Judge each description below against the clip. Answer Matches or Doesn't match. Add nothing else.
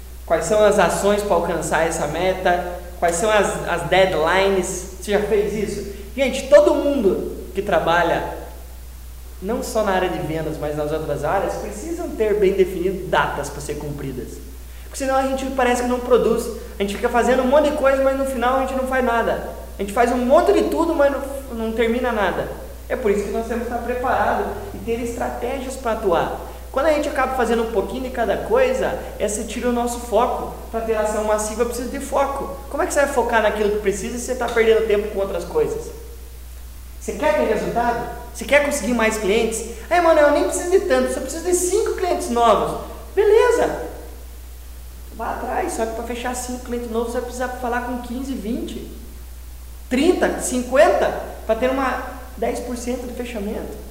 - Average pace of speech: Doesn't match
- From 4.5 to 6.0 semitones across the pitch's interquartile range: Matches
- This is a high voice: Matches